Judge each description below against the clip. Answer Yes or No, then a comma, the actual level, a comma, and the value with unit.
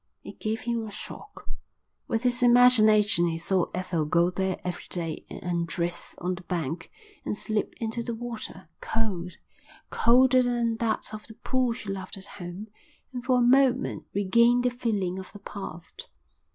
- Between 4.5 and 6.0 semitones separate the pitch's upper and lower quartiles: Yes, average, 4.9 semitones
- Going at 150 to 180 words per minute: Yes, average, 165 wpm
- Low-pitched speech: No, high, 215 Hz